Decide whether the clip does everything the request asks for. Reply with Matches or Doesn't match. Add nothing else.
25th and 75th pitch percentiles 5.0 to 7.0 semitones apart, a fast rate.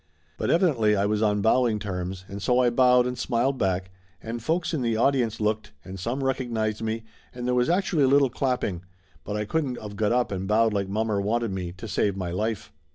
Doesn't match